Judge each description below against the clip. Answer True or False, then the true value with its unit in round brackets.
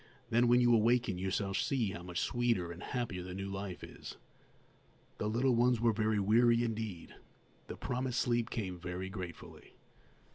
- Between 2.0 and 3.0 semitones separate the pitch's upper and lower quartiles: False (4.2 semitones)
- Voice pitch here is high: False (110 Hz)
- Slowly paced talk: False (170 wpm)